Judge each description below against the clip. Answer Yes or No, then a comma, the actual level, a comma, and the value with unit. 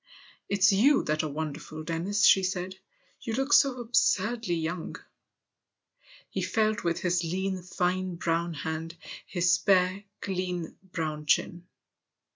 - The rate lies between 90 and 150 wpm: Yes, slow, 135 wpm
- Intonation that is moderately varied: Yes, average, 3.1 semitones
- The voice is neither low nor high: Yes, medium, 180 Hz